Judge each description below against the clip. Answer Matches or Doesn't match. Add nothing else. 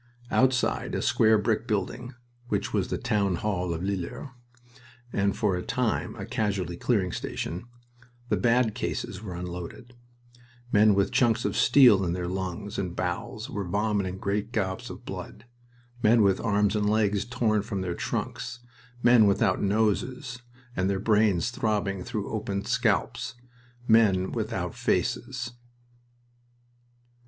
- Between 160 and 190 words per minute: Doesn't match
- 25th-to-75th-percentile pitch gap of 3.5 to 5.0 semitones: Doesn't match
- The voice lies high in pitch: Doesn't match